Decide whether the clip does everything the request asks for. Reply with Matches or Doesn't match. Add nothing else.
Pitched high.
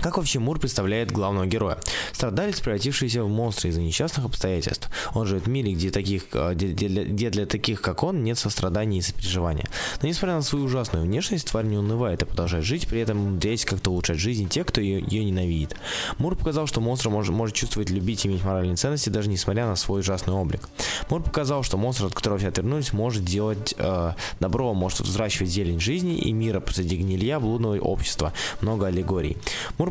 Doesn't match